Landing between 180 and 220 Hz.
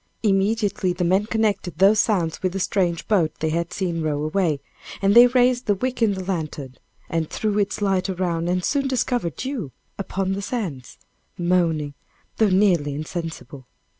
Yes: medium, 185 Hz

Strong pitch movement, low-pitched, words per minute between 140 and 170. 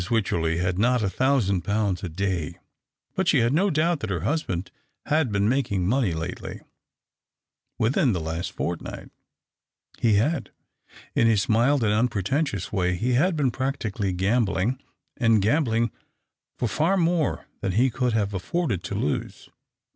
Yes: wide, 5.9 semitones; low, 115 Hz; average, 155 wpm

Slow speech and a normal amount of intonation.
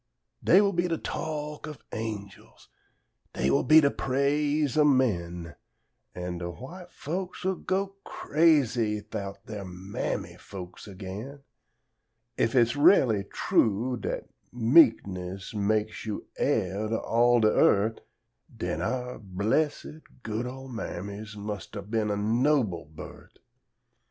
No: slow, 125 wpm; wide, 6.3 semitones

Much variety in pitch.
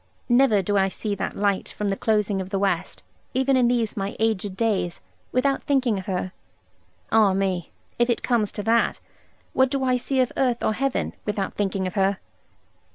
No: average, 4.0 semitones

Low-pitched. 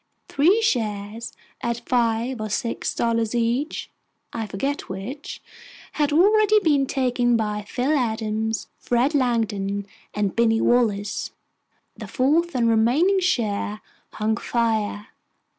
No: high, 235 Hz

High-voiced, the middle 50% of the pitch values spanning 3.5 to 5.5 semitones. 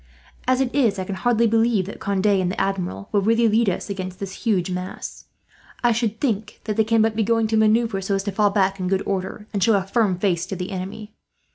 No: high, 205 Hz; average, 2.8 semitones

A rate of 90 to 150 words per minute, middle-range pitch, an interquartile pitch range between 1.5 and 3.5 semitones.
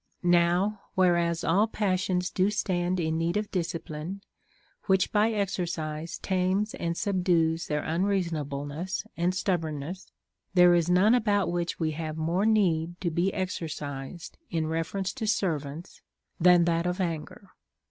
Yes: average, 145 wpm; medium, 175 Hz; average, 2.7 semitones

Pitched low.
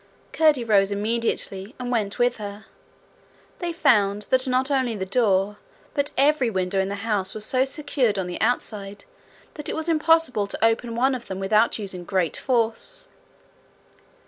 No: high, 225 Hz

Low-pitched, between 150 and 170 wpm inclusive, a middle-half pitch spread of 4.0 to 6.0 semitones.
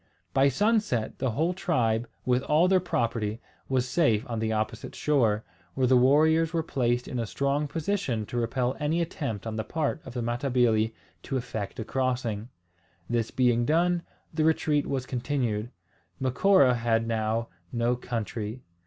Yes: low, 125 Hz; average, 160 wpm; average, 4.4 semitones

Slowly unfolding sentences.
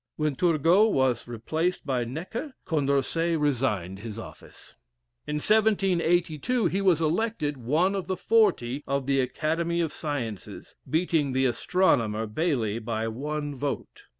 Yes: slow, 130 wpm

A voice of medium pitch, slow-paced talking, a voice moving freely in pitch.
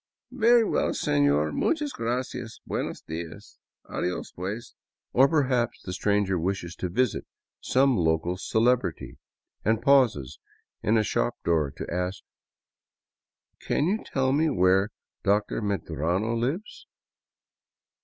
No: low, 105 Hz; slow, 125 wpm; wide, 6.5 semitones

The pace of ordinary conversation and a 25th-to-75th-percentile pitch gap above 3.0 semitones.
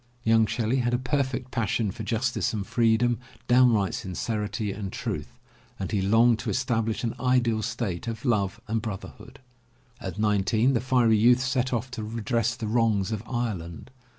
No: average, 170 wpm; narrow, 2.5 semitones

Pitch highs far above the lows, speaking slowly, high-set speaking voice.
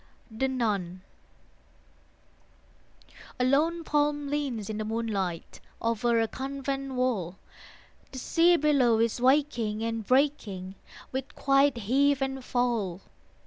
No: average, 4.1 semitones; slow, 110 wpm; very high, 250 Hz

